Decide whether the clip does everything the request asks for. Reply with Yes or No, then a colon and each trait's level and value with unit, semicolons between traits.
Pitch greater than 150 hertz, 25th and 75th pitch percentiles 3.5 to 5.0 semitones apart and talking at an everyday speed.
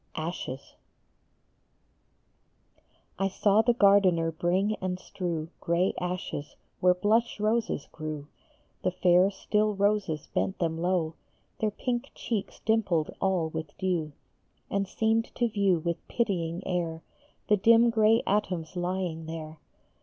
No: medium, 185 Hz; average, 4.3 semitones; slow, 120 wpm